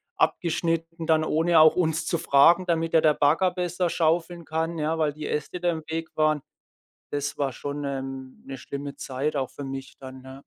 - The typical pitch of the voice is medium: Yes, medium, 155 Hz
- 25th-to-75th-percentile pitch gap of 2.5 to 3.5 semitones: Yes, average, 2.8 semitones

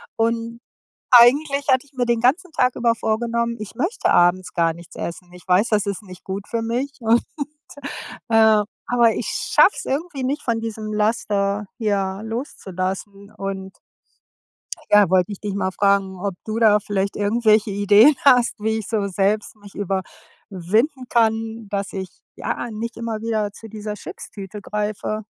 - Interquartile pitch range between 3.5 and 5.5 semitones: No, average, 2.8 semitones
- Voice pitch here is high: Yes, high, 215 Hz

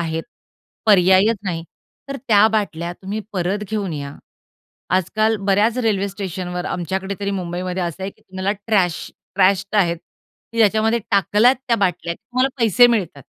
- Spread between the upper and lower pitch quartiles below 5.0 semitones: Yes, average, 3.3 semitones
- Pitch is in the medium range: No, high, 195 Hz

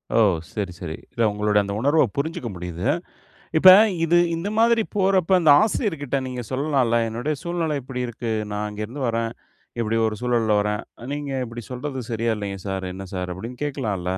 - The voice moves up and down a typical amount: No, wide, 5.9 semitones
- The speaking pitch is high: No, low, 120 Hz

